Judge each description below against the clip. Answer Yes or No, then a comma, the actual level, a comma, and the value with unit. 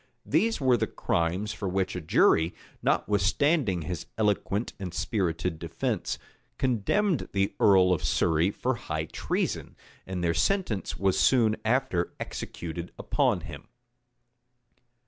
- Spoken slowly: Yes, slow, 125 wpm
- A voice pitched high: No, very low, 95 Hz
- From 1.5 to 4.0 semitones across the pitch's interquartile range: No, average, 5.1 semitones